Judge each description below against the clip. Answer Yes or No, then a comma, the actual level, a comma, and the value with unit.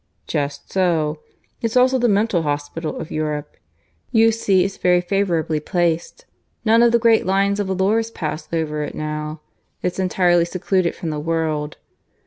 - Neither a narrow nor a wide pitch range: Yes, average, 4.6 semitones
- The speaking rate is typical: Yes, average, 155 wpm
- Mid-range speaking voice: Yes, medium, 175 Hz